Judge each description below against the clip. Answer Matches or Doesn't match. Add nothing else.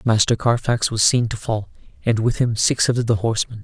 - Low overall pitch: Matches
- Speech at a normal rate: Doesn't match